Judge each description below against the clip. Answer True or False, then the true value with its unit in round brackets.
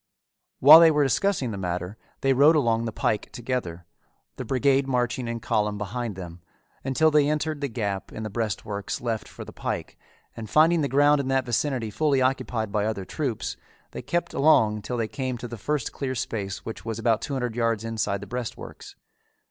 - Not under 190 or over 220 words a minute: True (195 wpm)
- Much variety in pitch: False (4.3 semitones)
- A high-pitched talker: False (120 Hz)